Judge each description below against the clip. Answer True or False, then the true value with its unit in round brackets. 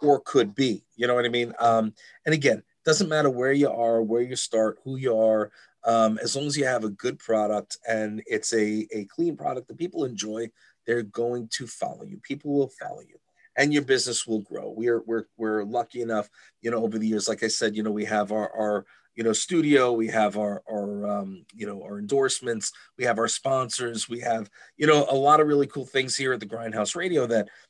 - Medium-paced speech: False (230 wpm)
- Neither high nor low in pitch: False (115 Hz)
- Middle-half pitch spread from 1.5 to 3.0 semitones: False (3.4 semitones)